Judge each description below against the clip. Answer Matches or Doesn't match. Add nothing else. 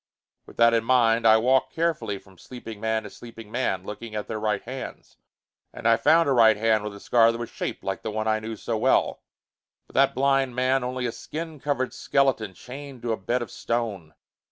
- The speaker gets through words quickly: Matches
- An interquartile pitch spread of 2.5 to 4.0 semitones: Matches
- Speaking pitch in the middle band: Doesn't match